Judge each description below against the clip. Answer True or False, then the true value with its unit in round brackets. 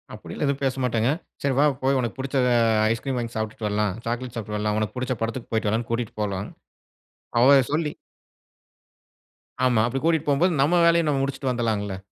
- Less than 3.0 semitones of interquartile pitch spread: False (3.8 semitones)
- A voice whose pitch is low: True (125 Hz)